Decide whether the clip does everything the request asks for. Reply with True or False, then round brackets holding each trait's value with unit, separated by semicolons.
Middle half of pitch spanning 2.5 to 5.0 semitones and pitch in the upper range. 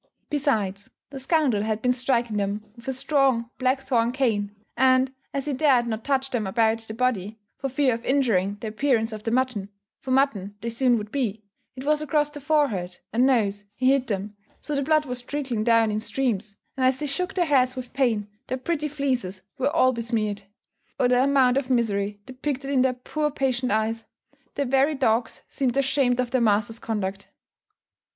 True (3.7 semitones; 250 Hz)